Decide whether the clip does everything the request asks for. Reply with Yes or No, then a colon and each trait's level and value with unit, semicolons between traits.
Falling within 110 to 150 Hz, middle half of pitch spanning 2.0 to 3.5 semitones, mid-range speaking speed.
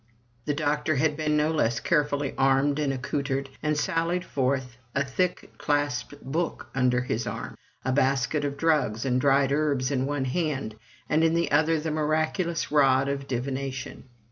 Yes: medium, 140 Hz; narrow, 2.5 semitones; average, 165 wpm